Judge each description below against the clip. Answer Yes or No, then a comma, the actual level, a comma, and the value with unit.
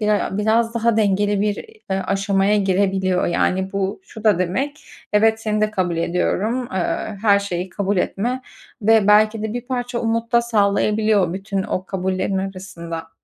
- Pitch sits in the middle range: No, high, 205 Hz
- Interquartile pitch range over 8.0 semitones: No, narrow, 2.6 semitones